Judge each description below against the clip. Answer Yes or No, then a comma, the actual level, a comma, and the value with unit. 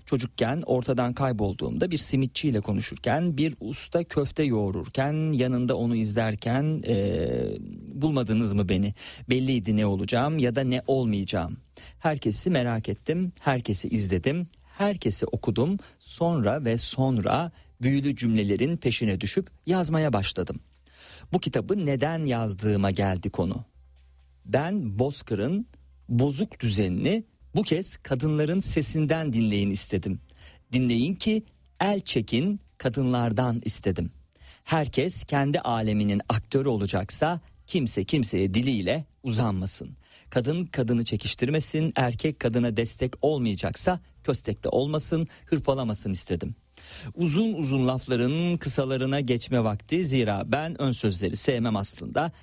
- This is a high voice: No, low, 125 Hz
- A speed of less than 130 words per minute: Yes, average, 110 wpm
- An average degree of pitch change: No, wide, 6.2 semitones